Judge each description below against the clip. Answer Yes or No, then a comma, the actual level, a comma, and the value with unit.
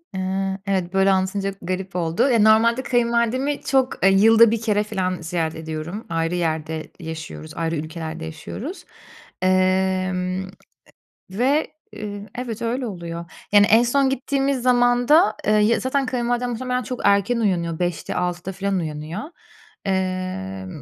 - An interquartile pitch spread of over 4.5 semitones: Yes, average, 4.9 semitones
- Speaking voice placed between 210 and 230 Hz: No, high, 195 Hz